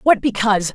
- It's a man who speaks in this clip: No, female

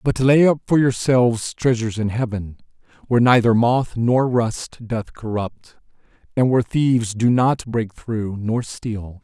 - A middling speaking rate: Yes, average, 155 wpm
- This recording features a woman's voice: No, male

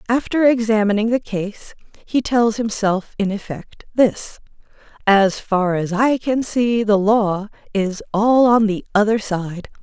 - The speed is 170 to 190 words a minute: No, average, 145 wpm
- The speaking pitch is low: No, high, 215 Hz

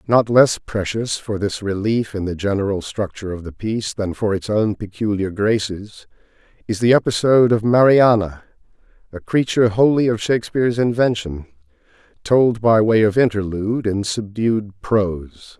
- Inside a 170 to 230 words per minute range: No, average, 145 wpm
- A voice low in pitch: Yes, low, 105 Hz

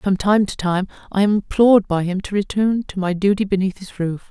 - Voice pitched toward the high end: Yes, high, 195 Hz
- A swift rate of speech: Yes, fast, 235 wpm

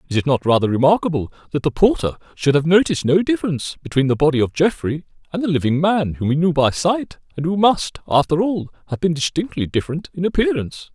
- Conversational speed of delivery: No, fast, 210 wpm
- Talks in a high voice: No, medium, 165 Hz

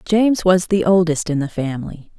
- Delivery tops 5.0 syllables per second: Yes, 5.4 syllables/s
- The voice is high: No, medium, 175 Hz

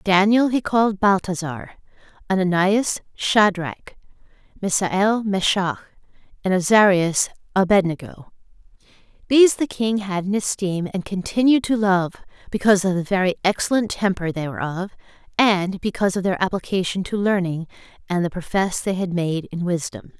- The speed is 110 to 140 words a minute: Yes, slow, 135 wpm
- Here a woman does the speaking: Yes, female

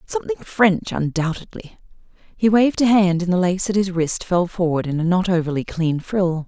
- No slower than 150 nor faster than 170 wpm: No, average, 195 wpm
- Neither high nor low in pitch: Yes, medium, 180 Hz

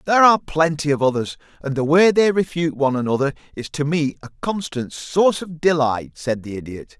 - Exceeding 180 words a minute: Yes, average, 195 wpm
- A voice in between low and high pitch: Yes, medium, 150 Hz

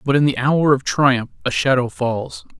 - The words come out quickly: Yes, fast, 210 wpm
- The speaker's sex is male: Yes, male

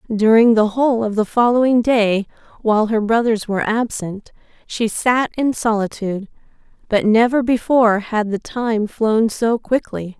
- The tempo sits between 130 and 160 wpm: Yes, average, 145 wpm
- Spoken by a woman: Yes, female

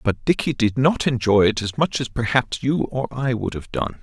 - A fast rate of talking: Yes, fast, 240 wpm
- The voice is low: Yes, low, 125 Hz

